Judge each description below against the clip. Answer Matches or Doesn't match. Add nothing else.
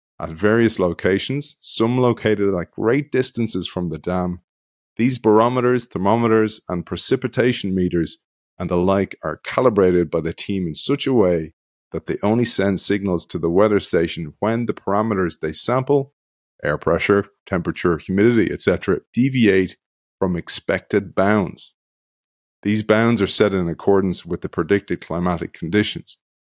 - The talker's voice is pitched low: Matches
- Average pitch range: Matches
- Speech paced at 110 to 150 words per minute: Matches